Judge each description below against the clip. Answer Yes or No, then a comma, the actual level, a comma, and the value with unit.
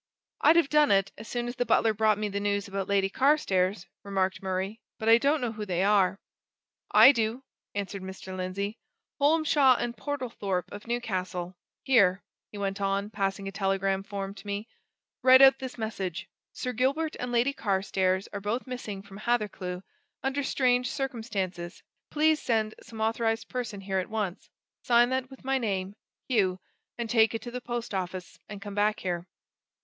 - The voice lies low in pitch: No, high, 210 Hz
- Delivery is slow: No, average, 175 wpm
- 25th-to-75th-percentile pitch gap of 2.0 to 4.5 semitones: Yes, average, 4.1 semitones